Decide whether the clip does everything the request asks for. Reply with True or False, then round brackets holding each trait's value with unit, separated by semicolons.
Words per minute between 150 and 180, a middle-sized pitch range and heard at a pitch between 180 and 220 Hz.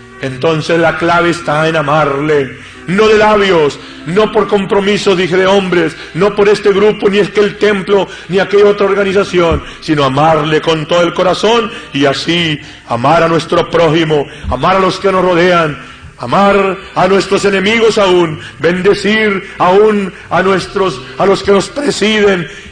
True (160 wpm; 4.0 semitones; 185 Hz)